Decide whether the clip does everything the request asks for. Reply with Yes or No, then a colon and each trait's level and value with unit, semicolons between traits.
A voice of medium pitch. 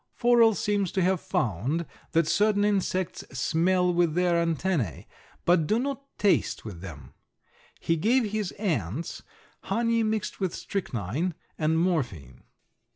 Yes: medium, 175 Hz